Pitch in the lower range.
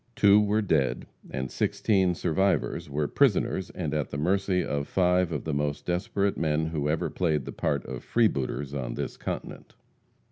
Yes: very low, 80 Hz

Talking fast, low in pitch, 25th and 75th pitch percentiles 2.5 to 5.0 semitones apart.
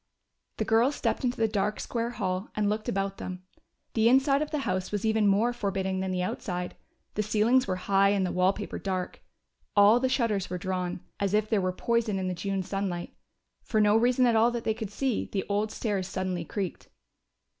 No: fast, 210 wpm; high, 205 Hz; average, 3.1 semitones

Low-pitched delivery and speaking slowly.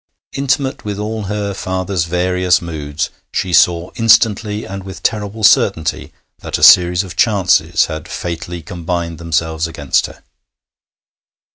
Yes: very low, 90 Hz; slow, 130 wpm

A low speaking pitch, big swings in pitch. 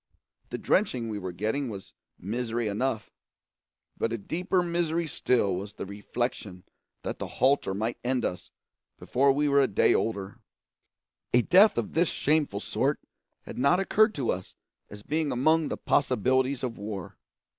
Yes: low, 125 Hz; wide, 6.0 semitones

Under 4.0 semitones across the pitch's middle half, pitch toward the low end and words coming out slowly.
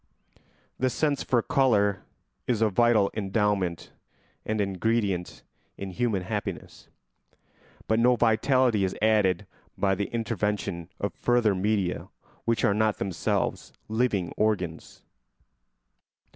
Yes: average, 3.0 semitones; low, 105 Hz; slow, 115 wpm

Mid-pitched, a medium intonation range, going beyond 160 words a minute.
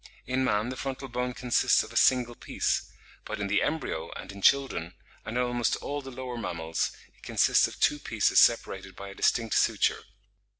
No: low, 120 Hz; average, 4.2 semitones; average, 190 wpm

